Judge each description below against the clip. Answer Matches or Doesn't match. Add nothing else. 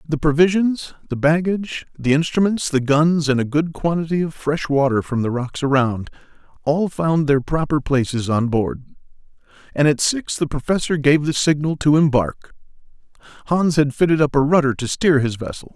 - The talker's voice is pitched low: Doesn't match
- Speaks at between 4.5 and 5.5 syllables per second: Matches